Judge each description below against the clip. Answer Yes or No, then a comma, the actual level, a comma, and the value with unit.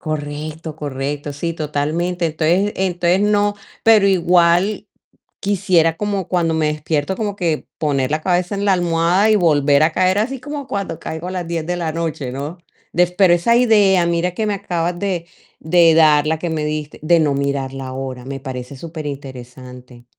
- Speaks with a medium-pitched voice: Yes, medium, 165 Hz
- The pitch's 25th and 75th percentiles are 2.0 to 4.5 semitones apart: Yes, average, 3.9 semitones